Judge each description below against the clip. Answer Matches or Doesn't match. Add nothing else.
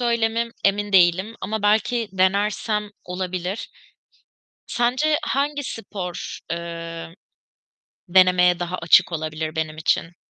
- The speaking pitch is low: Doesn't match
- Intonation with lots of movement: Doesn't match